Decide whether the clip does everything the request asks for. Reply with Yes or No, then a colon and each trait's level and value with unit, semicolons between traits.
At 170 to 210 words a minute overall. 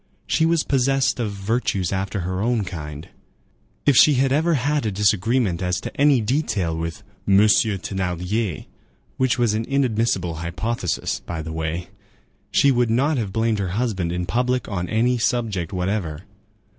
No: average, 150 wpm